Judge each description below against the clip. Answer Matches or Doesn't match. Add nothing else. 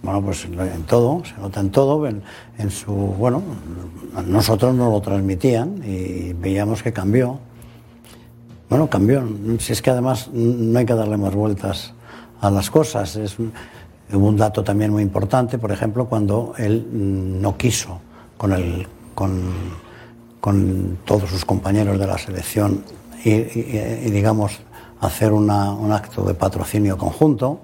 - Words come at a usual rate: Matches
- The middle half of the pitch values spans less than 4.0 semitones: Matches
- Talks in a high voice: Doesn't match